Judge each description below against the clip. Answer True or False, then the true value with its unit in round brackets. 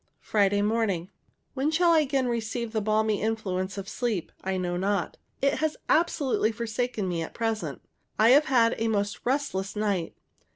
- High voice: True (220 Hz)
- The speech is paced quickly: False (165 wpm)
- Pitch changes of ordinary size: True (3.9 semitones)